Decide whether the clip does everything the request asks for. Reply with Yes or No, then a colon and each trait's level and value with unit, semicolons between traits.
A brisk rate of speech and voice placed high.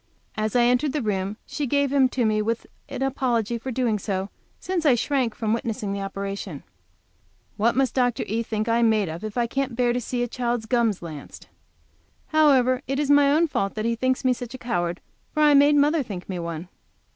Yes: fast, 215 wpm; high, 235 Hz